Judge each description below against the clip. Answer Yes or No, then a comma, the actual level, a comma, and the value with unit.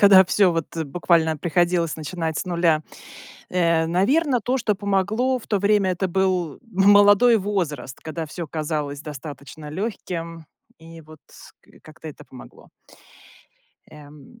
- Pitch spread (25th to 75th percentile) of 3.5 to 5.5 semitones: Yes, average, 4.2 semitones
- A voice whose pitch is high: No, medium, 170 Hz